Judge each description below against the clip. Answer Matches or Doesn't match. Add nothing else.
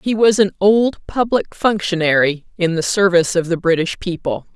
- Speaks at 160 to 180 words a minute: Matches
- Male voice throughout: Doesn't match